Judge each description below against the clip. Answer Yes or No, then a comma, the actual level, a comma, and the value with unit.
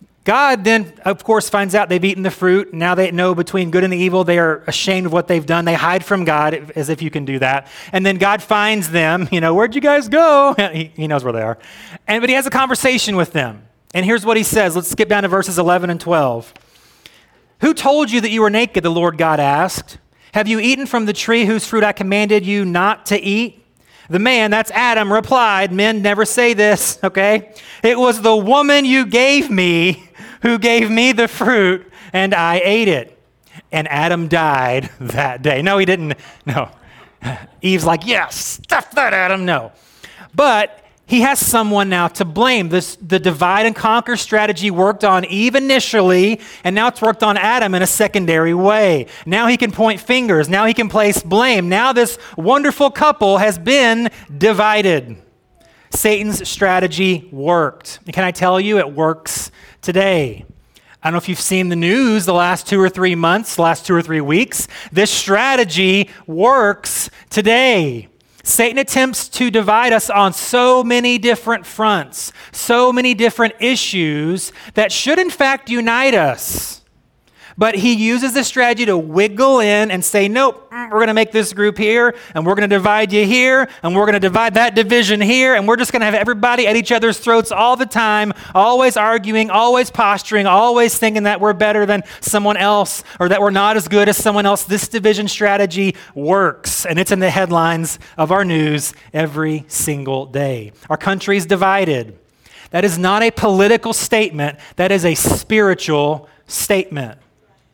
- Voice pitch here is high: Yes, high, 205 Hz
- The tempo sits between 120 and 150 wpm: No, average, 185 wpm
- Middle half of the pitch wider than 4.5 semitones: No, average, 4.2 semitones